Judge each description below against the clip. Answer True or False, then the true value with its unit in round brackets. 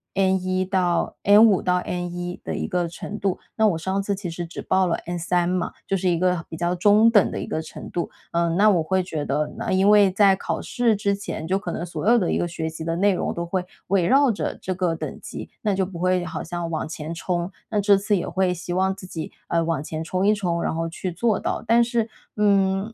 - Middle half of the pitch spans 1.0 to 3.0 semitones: True (2.7 semitones)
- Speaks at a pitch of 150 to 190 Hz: True (185 Hz)